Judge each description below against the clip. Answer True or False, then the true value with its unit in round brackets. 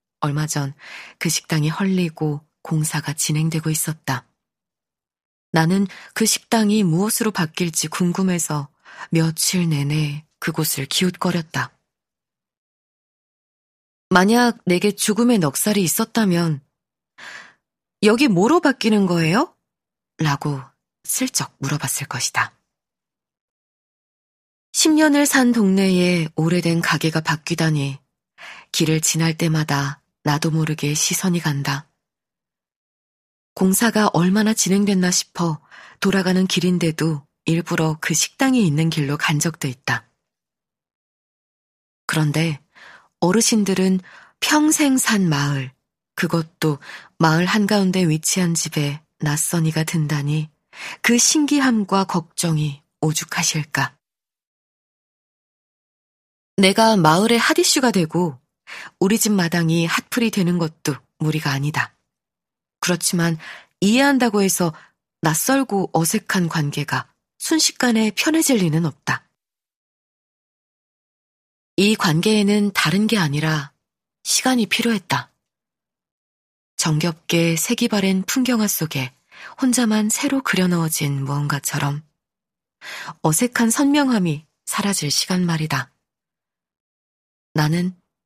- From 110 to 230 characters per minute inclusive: True (220 characters per minute)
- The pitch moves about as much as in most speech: True (4.9 semitones)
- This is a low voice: False (170 Hz)